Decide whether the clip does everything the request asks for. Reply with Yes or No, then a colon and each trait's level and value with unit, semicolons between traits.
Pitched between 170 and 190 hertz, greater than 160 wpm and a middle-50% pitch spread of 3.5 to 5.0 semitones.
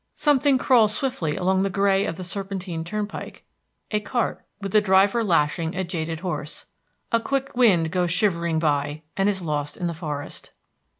Yes: medium, 185 Hz; average, 170 wpm; average, 4.4 semitones